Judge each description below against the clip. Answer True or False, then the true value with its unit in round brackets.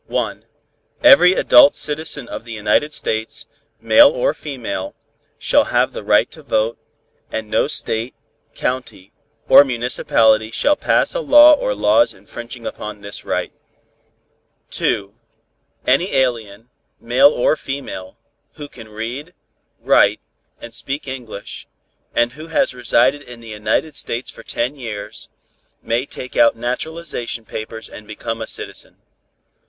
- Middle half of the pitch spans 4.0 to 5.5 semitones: True (4.4 semitones)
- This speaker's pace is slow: True (130 wpm)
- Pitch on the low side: True (120 Hz)